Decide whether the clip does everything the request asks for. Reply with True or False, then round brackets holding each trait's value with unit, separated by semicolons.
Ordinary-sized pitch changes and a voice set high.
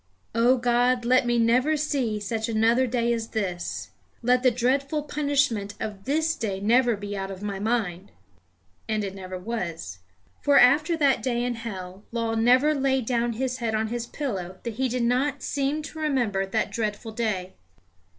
True (3.7 semitones; 235 Hz)